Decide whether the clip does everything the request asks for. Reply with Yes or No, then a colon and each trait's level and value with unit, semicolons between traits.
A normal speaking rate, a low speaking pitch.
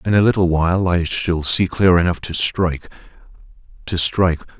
Yes: average, 155 wpm; very low, 90 Hz